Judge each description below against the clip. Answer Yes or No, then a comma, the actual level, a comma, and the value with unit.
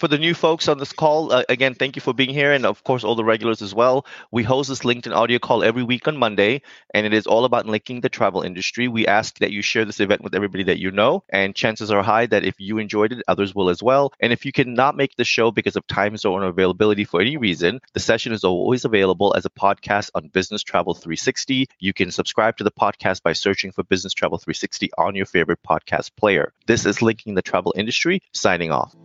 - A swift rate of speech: Yes, fast, 245 wpm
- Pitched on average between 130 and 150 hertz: No, low, 110 Hz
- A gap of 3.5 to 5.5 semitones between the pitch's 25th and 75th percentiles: Yes, average, 4.6 semitones